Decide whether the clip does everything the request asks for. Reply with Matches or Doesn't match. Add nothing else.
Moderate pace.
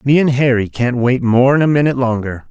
Doesn't match